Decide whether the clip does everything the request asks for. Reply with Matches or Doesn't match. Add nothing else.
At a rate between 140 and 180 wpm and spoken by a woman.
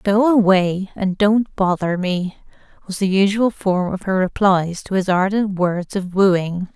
Matches